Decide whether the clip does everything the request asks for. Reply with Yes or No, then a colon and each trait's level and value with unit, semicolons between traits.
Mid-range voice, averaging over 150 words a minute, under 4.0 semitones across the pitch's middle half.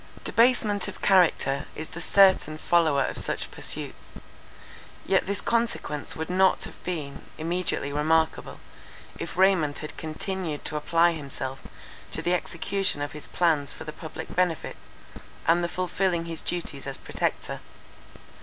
No: medium, 165 Hz; average, 140 wpm; average, 3.4 semitones